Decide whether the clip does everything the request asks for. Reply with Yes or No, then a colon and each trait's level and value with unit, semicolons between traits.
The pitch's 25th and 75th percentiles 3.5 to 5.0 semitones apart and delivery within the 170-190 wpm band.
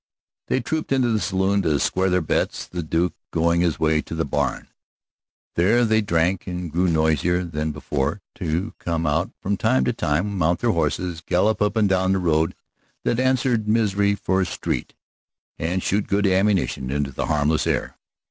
Yes: average, 4.2 semitones; average, 180 wpm